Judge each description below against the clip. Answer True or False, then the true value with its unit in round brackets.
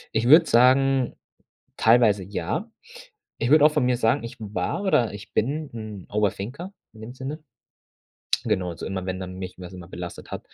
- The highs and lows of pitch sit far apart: True (5.8 semitones)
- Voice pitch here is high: False (115 Hz)